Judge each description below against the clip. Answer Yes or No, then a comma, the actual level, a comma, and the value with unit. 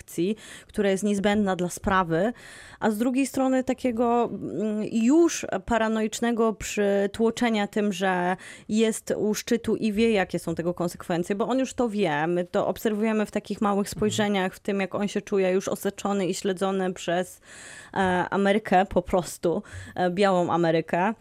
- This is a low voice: No, high, 205 Hz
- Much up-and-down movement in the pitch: No, average, 3.1 semitones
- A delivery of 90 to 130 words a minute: No, average, 145 wpm